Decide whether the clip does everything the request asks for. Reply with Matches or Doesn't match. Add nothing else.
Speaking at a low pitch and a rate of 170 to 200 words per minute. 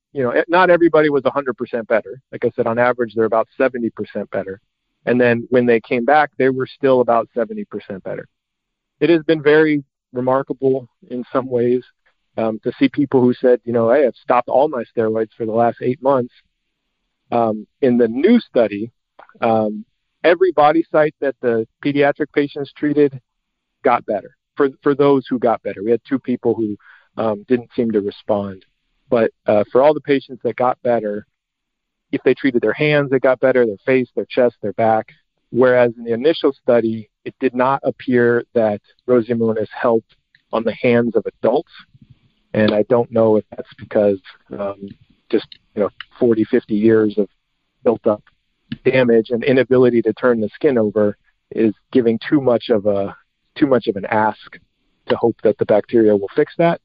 Matches